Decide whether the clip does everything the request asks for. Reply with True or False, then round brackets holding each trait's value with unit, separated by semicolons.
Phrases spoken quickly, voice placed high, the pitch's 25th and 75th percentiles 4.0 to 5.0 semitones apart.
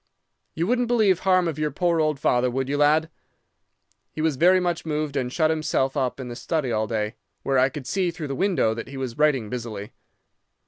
False (215 wpm; 150 Hz; 4.6 semitones)